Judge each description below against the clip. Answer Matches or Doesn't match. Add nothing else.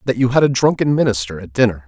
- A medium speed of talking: Doesn't match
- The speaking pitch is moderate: Doesn't match